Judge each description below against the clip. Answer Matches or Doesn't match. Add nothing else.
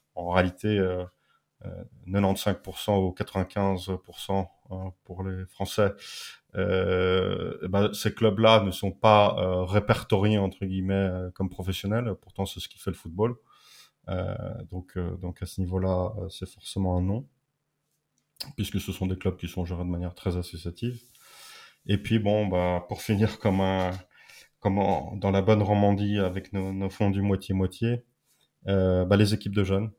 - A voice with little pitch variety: Matches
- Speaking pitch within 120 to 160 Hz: Doesn't match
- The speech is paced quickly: Doesn't match